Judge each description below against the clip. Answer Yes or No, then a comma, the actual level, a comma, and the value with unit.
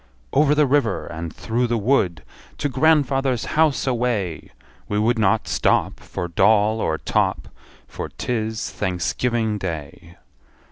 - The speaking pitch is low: Yes, low, 110 Hz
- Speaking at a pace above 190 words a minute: No, slow, 135 wpm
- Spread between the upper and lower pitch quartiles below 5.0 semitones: No, wide, 5.5 semitones